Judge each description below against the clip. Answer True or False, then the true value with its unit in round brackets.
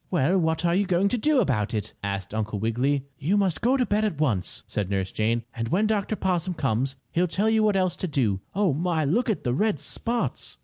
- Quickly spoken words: True (230 wpm)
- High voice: False (165 Hz)